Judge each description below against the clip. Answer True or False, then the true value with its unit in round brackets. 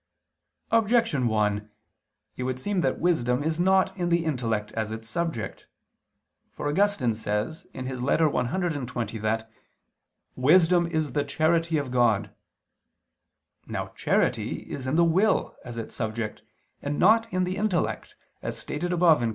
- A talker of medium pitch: True (145 Hz)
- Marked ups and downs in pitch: True (6.9 semitones)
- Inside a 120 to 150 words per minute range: True (140 wpm)